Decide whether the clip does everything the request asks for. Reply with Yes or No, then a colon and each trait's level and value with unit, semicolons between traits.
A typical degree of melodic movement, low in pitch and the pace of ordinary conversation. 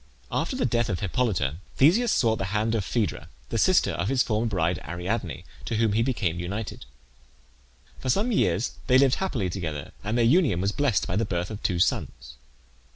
No: wide, 6.0 semitones; low, 105 Hz; average, 190 wpm